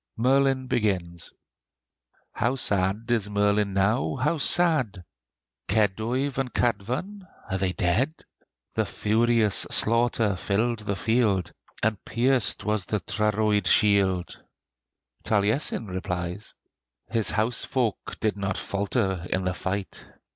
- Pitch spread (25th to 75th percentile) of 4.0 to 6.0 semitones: No, average, 3.6 semitones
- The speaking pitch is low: Yes, low, 105 Hz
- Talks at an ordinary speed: No, slow, 110 wpm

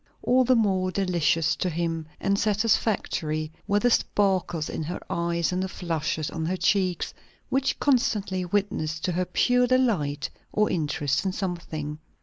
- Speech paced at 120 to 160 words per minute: Yes, average, 150 wpm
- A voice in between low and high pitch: Yes, medium, 180 Hz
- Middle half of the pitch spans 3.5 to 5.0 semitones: Yes, average, 4.2 semitones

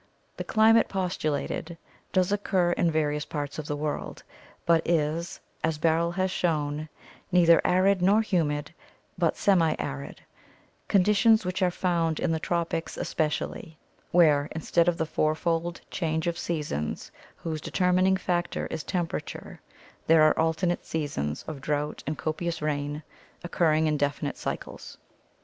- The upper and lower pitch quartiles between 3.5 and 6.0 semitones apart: No, average, 2.7 semitones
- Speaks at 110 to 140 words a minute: Yes, slow, 135 wpm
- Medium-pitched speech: Yes, medium, 165 Hz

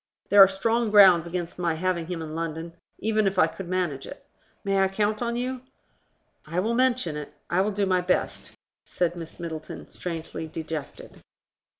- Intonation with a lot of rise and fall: No, average, 3.7 semitones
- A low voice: No, medium, 185 Hz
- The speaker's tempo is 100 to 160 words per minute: No, average, 180 wpm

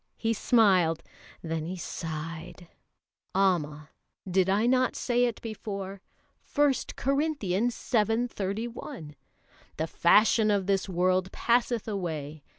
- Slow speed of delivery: Yes, slow, 110 wpm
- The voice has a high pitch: Yes, high, 195 Hz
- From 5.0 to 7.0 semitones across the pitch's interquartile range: Yes, average, 5.3 semitones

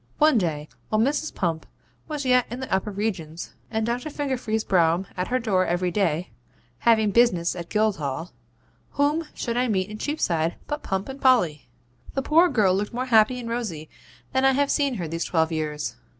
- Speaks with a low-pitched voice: No, high, 215 Hz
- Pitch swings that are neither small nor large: No, wide, 6.7 semitones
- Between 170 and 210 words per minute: Yes, average, 185 wpm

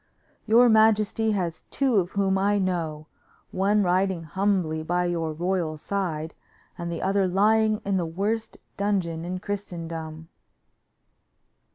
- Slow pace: Yes, slow, 130 wpm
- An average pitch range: Yes, average, 3.4 semitones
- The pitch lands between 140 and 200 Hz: Yes, medium, 185 Hz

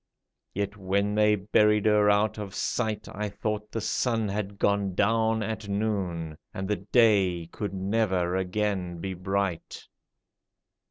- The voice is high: No, low, 100 Hz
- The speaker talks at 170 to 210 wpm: No, average, 145 wpm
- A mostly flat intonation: Yes, narrow, 1.9 semitones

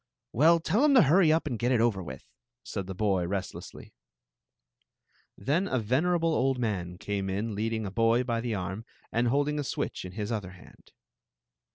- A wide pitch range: Yes, wide, 6.3 semitones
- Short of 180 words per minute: No, average, 185 wpm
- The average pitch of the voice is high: No, low, 115 Hz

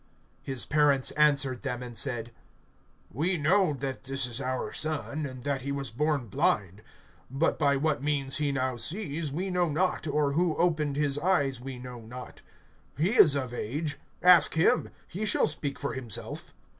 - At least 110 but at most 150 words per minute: No, average, 170 wpm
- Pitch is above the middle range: No, medium, 140 Hz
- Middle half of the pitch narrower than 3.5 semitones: Yes, average, 3.1 semitones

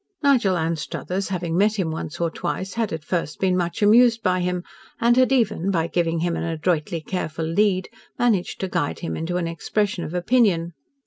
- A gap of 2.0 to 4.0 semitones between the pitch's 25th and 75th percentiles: Yes, average, 3.7 semitones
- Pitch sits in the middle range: Yes, medium, 180 Hz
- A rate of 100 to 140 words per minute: No, average, 190 wpm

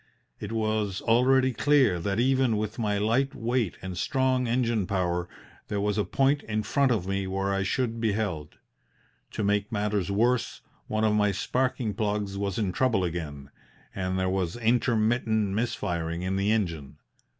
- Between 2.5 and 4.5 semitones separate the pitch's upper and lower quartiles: Yes, average, 3.5 semitones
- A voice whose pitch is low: Yes, low, 105 Hz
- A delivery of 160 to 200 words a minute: Yes, average, 165 wpm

